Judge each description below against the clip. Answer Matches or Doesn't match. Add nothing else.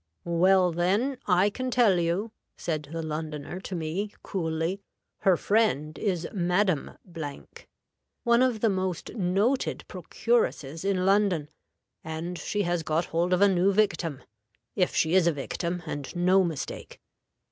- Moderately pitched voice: Matches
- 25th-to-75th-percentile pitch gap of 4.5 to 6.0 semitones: Doesn't match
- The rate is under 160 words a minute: Matches